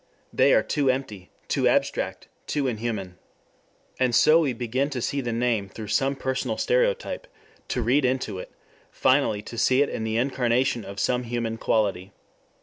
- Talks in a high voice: No, low, 125 Hz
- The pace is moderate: Yes, average, 165 wpm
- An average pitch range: Yes, average, 3.4 semitones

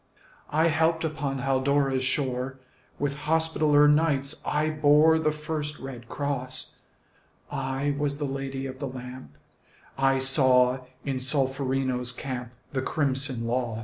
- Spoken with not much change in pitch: Yes, narrow, 2.3 semitones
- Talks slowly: Yes, slow, 125 wpm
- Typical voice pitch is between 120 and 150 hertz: Yes, low, 135 Hz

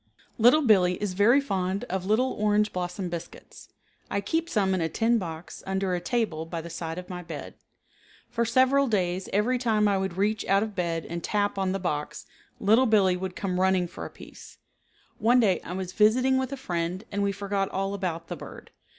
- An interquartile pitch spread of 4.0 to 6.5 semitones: No, average, 3.4 semitones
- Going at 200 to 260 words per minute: Yes, fast, 205 wpm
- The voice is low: No, high, 195 Hz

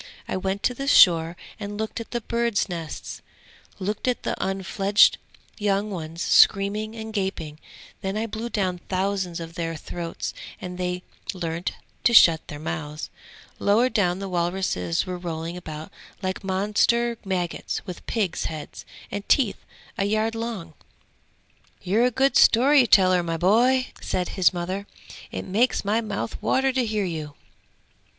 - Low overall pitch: No, high, 195 Hz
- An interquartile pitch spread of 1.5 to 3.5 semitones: No, average, 4.0 semitones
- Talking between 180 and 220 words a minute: No, average, 150 wpm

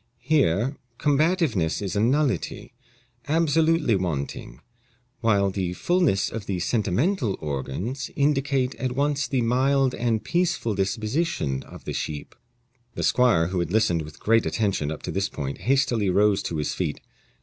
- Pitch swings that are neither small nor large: No, wide, 7.1 semitones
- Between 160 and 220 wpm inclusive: No, average, 145 wpm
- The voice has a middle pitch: No, low, 115 Hz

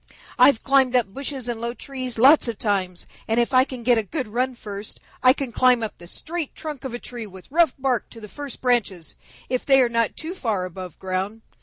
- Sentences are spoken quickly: Yes, fast, 225 wpm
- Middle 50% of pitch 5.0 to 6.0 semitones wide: No, average, 3.9 semitones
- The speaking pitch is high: Yes, high, 240 Hz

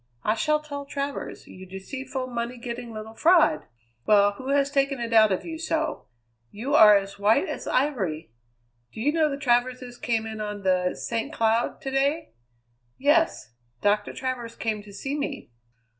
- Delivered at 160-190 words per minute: Yes, average, 170 wpm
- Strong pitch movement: No, average, 4.8 semitones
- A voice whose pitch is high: Yes, high, 240 Hz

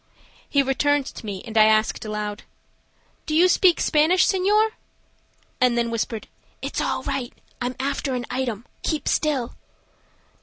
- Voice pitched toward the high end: Yes, very high, 260 Hz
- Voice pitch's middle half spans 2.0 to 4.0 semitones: No, average, 5.1 semitones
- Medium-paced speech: Yes, average, 145 wpm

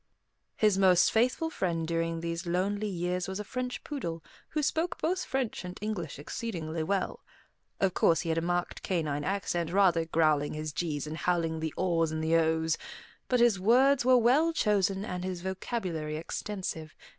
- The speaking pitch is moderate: Yes, medium, 180 Hz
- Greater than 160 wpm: Yes, average, 170 wpm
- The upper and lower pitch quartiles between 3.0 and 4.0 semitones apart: No, average, 4.5 semitones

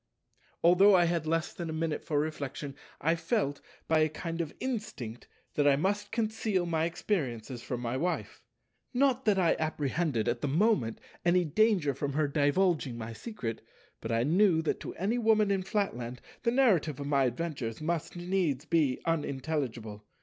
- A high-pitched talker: No, medium, 160 Hz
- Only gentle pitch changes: No, wide, 5.6 semitones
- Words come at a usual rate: Yes, average, 170 wpm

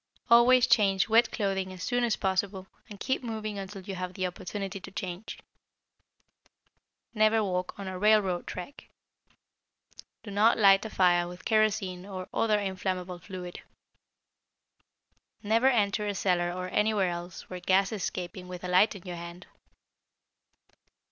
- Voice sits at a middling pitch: No, high, 195 Hz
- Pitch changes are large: No, average, 2.8 semitones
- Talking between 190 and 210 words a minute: No, average, 145 wpm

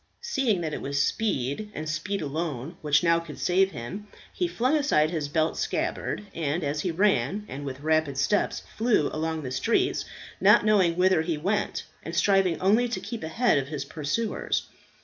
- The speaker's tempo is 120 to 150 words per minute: No, average, 180 wpm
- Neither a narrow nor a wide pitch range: No, wide, 5.8 semitones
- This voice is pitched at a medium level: Yes, medium, 165 Hz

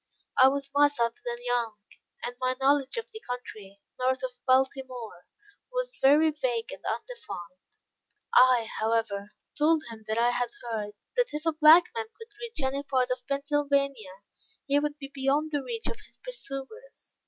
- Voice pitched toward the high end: Yes, very high, 270 Hz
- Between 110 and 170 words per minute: Yes, average, 165 wpm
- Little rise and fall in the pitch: No, average, 3.9 semitones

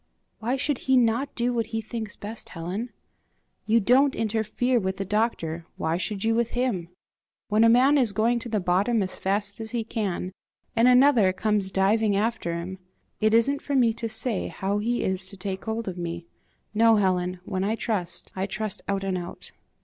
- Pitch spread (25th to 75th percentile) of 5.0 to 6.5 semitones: No, average, 3.6 semitones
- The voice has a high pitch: Yes, high, 215 Hz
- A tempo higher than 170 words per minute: Yes, average, 195 wpm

